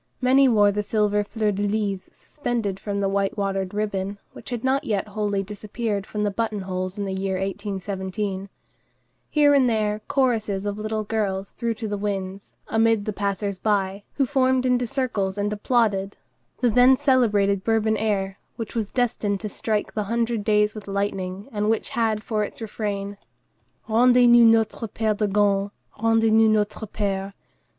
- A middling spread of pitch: No, narrow, 2.2 semitones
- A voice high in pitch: Yes, high, 210 Hz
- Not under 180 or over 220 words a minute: No, average, 170 wpm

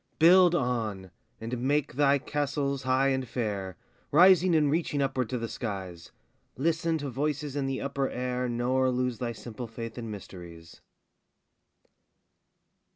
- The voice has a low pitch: Yes, low, 130 Hz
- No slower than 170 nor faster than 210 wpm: No, average, 140 wpm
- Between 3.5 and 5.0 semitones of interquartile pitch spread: Yes, average, 3.9 semitones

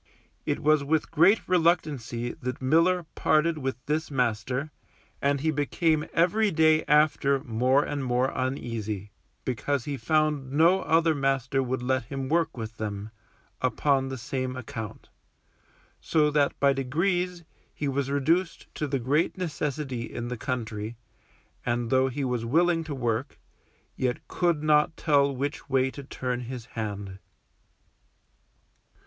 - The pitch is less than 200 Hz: Yes, medium, 140 Hz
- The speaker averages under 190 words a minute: Yes, average, 140 wpm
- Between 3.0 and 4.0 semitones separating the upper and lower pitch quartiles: Yes, average, 3.7 semitones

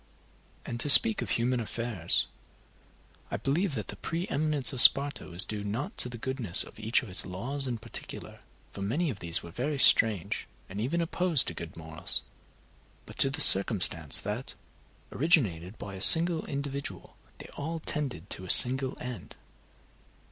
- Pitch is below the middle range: Yes, low, 120 Hz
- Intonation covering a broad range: Yes, wide, 6.5 semitones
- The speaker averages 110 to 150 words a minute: No, average, 170 wpm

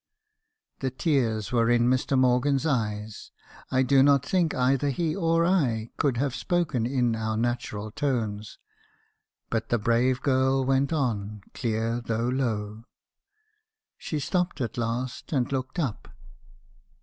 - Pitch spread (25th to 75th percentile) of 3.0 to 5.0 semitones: Yes, average, 3.4 semitones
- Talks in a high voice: No, low, 125 Hz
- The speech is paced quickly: No, slow, 135 wpm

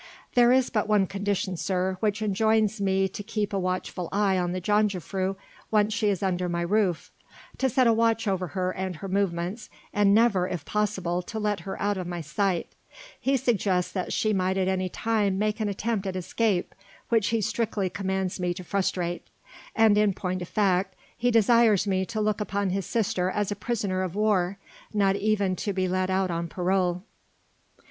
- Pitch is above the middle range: Yes, high, 195 Hz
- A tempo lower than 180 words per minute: No, average, 190 wpm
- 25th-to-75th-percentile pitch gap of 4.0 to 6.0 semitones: No, narrow, 2.5 semitones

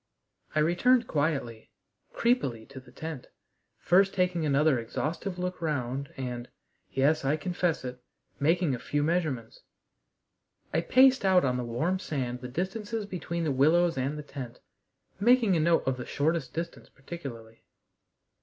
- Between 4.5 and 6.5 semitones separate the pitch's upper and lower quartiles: Yes, wide, 5.5 semitones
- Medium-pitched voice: Yes, medium, 155 Hz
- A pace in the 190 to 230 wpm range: No, average, 145 wpm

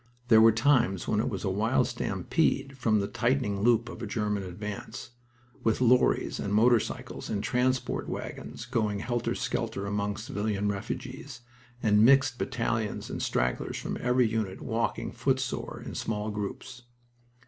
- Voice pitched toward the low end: Yes, low, 110 Hz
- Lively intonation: No, average, 3.0 semitones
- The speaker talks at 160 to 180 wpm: No, average, 150 wpm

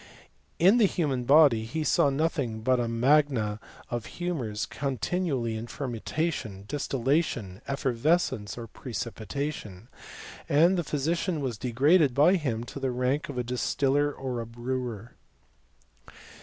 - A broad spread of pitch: No, average, 4.5 semitones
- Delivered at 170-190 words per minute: No, average, 145 wpm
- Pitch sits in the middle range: No, low, 130 Hz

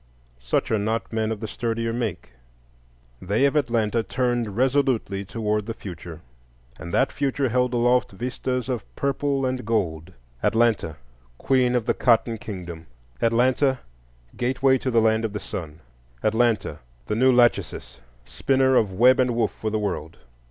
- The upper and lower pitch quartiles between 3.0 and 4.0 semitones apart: Yes, average, 3.5 semitones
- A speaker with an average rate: Yes, average, 150 wpm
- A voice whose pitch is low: Yes, low, 115 Hz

